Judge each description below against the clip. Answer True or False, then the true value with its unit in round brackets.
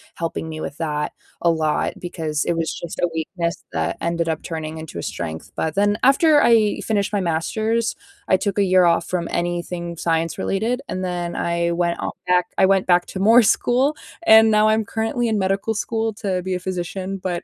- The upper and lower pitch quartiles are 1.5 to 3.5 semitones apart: False (4.0 semitones)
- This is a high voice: False (180 Hz)